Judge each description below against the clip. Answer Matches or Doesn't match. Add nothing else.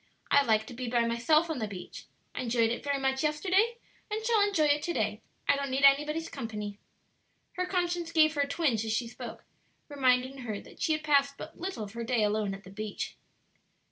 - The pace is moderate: Doesn't match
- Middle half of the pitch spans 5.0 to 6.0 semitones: Matches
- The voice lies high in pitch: Matches